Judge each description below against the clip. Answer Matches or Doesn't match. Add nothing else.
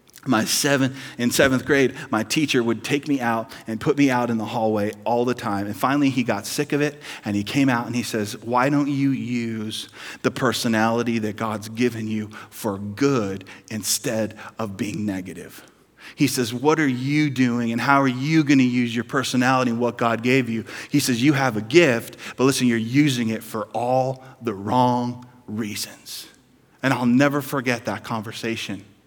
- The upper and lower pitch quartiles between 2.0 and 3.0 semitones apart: Doesn't match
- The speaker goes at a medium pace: Matches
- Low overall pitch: Matches